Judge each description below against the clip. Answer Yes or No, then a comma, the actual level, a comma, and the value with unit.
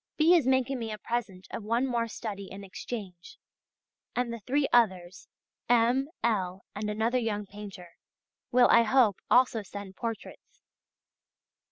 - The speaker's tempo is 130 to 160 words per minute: Yes, average, 145 wpm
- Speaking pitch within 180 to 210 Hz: No, high, 225 Hz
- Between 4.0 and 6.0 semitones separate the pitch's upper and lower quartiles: No, average, 3.5 semitones